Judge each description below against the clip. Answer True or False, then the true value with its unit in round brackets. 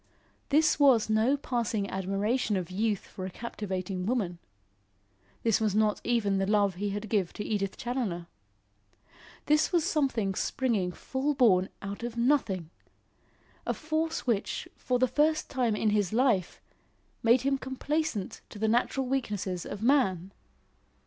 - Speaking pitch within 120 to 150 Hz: False (220 Hz)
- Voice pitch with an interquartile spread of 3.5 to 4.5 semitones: False (5.0 semitones)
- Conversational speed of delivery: True (145 wpm)